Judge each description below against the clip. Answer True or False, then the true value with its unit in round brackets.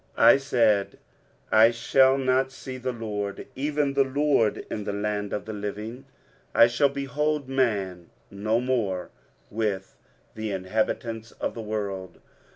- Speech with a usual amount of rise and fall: True (4.3 semitones)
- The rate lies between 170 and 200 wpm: False (145 wpm)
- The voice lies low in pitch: True (115 Hz)